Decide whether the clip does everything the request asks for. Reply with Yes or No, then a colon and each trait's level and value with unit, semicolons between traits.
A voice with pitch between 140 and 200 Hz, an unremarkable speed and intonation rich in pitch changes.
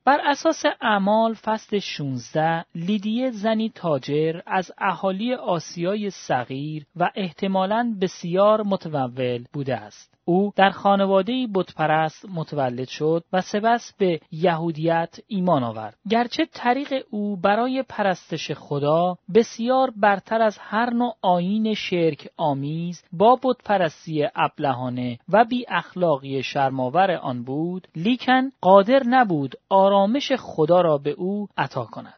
Yes: high, 190 Hz; average, 115 wpm; wide, 5.9 semitones